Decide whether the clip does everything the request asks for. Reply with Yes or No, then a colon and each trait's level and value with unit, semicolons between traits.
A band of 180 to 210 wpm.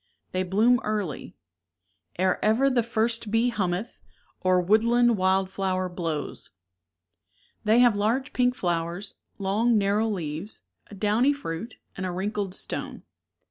No: slow, 135 wpm